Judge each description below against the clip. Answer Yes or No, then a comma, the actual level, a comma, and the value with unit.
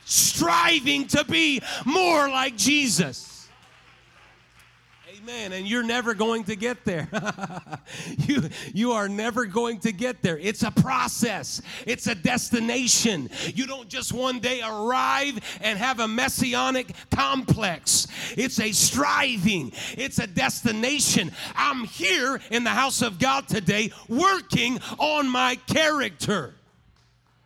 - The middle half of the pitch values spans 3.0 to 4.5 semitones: Yes, average, 3.9 semitones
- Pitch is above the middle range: Yes, high, 235 Hz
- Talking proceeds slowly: Yes, slow, 125 wpm